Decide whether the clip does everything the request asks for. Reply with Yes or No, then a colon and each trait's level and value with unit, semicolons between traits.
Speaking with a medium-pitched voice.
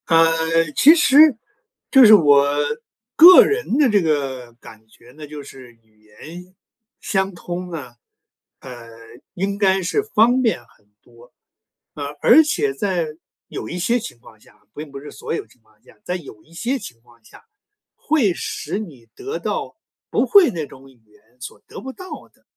Yes: medium, 165 Hz